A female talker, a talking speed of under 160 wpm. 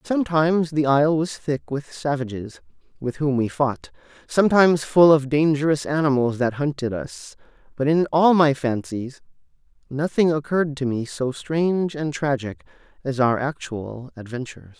No: male; average, 145 wpm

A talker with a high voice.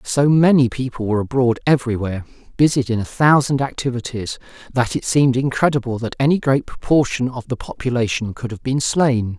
No: low, 125 Hz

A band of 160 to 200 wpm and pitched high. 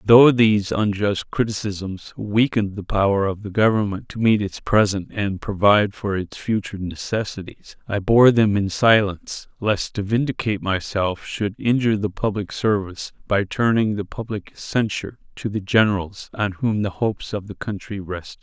No: average, 165 wpm; low, 105 Hz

